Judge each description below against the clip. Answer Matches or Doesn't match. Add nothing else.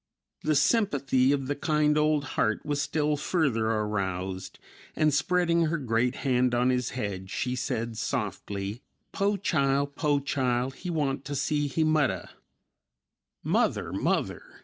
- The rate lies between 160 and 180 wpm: Doesn't match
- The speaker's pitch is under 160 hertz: Matches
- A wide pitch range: Doesn't match